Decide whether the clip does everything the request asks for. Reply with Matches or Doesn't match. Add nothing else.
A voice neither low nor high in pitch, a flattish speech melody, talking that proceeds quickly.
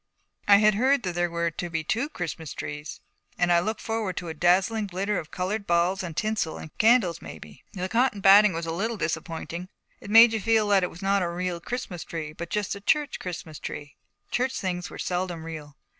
Doesn't match